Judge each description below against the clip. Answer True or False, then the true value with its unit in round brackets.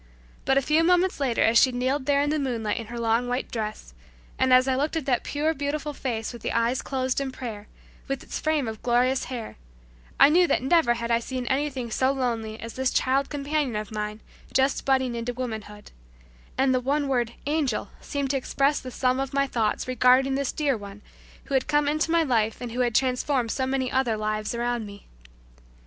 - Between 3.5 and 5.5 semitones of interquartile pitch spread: False (3.0 semitones)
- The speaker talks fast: True (215 wpm)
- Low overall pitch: False (255 Hz)